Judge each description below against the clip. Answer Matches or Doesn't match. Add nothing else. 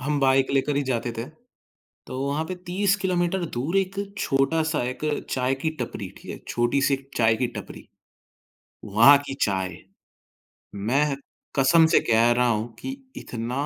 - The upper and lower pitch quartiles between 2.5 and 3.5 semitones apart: Doesn't match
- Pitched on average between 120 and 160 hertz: Matches